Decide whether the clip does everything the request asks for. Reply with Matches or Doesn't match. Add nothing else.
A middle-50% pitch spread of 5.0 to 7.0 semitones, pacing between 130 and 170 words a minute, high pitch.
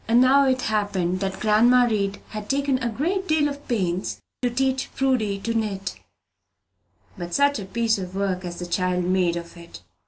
Doesn't match